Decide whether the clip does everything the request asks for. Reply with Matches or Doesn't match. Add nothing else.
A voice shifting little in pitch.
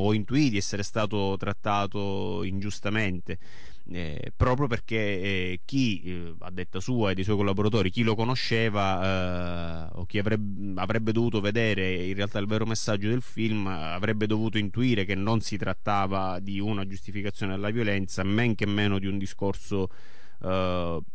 Matches